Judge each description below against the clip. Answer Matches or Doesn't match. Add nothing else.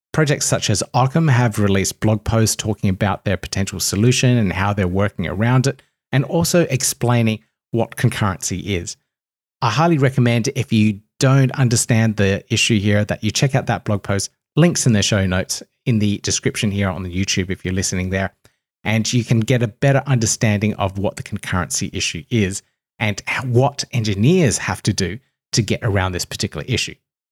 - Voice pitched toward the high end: Doesn't match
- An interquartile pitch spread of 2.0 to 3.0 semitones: Doesn't match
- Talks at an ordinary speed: Matches